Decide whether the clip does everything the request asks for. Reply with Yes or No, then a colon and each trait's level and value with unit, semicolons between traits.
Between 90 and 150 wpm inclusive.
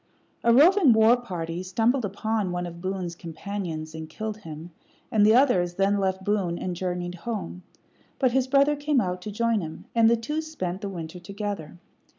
No: average, 180 wpm